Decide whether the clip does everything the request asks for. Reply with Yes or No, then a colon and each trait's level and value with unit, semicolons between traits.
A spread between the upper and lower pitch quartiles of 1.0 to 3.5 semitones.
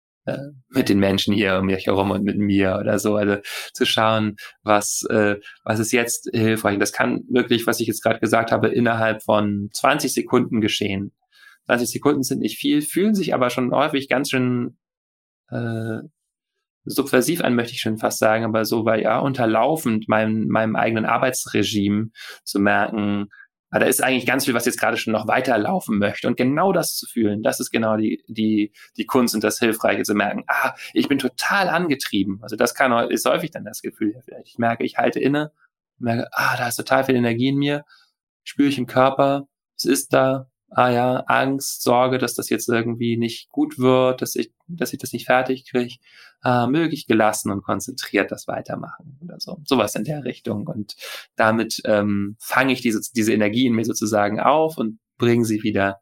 Yes: average, 3.2 semitones